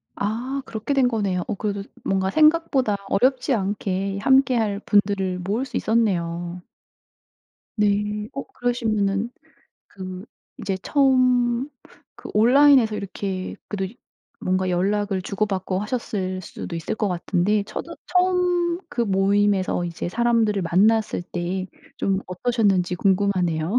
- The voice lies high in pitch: Yes, high, 205 Hz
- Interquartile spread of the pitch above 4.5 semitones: No, average, 4.1 semitones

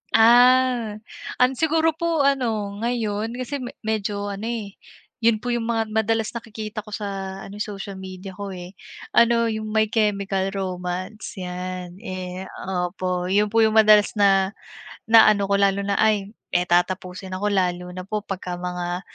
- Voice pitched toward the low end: No, high, 205 Hz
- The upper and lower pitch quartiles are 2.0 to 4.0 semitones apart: Yes, average, 3.0 semitones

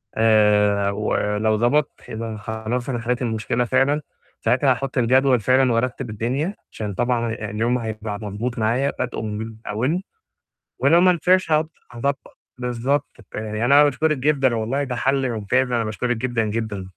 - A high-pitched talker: No, low, 120 Hz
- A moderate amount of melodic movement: Yes, average, 3.5 semitones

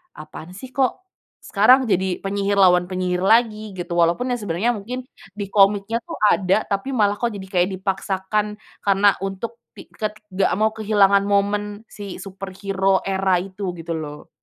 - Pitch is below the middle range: No, high, 200 Hz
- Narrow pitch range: Yes, narrow, 2.1 semitones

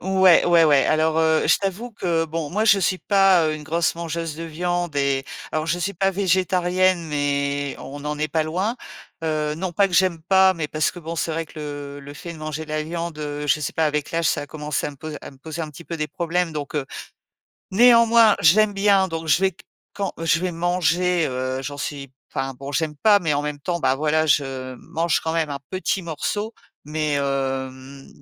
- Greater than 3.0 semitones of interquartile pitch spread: Yes, average, 3.4 semitones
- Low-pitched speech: No, medium, 160 Hz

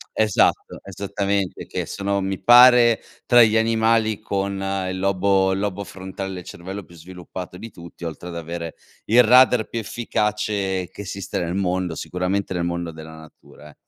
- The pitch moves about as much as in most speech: Yes, average, 3.1 semitones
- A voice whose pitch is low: Yes, very low, 95 Hz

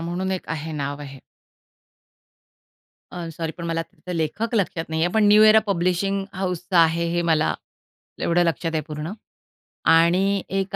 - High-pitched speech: No, medium, 170 Hz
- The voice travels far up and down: No, average, 2.9 semitones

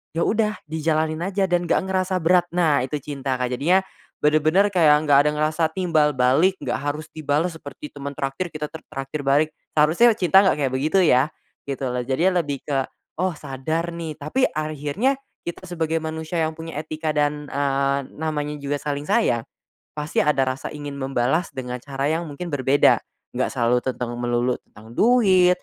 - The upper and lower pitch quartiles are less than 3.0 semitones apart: No, average, 3.5 semitones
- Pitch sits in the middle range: Yes, medium, 150 Hz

